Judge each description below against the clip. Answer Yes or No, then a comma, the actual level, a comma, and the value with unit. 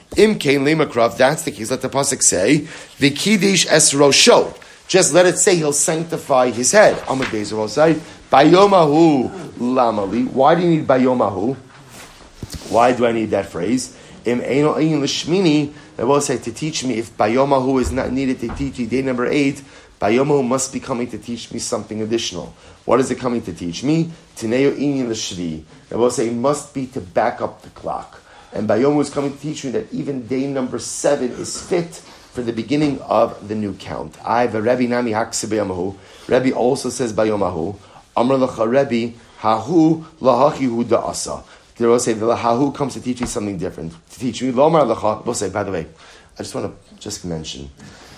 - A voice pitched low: Yes, low, 130 Hz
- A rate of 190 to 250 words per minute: No, average, 175 wpm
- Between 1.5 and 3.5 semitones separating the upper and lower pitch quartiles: No, average, 4.1 semitones